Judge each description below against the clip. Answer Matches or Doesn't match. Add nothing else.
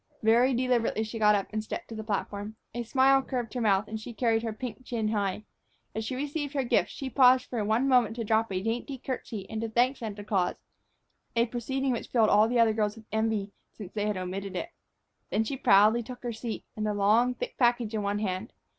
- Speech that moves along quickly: Matches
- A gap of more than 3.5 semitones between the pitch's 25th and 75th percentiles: Doesn't match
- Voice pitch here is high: Matches